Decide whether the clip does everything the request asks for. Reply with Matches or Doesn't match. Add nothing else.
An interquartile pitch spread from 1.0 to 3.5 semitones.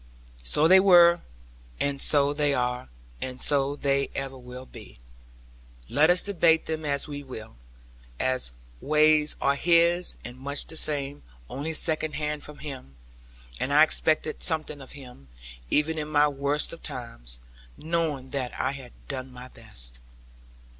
Matches